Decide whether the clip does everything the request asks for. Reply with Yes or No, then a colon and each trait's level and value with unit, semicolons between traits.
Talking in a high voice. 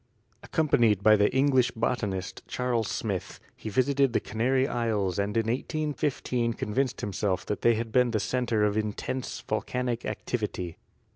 No: low, 115 Hz